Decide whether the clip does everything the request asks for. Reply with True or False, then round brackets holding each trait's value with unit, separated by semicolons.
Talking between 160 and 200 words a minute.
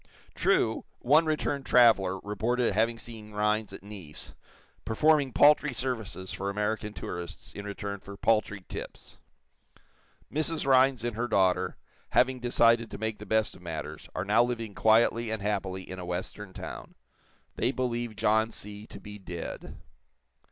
False (150 wpm)